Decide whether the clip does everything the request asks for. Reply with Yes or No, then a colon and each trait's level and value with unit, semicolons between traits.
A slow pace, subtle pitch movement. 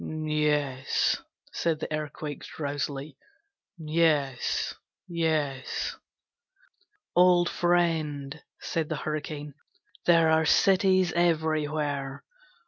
Yes: slow, 75 wpm; narrow, 2.3 semitones